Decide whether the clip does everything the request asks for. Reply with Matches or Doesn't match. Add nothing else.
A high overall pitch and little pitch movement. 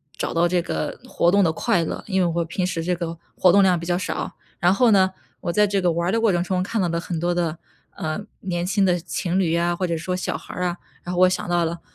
Doesn't match